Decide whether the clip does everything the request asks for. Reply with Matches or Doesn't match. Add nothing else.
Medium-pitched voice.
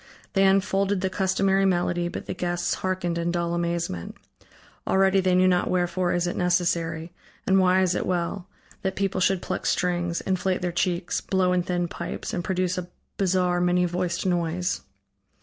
Matches